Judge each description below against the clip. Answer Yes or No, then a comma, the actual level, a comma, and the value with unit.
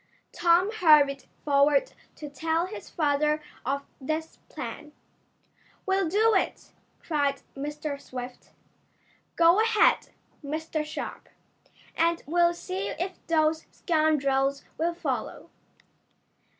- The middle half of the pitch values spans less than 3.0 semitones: No, average, 3.3 semitones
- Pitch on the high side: Yes, very high, 310 Hz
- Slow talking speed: Yes, slow, 100 wpm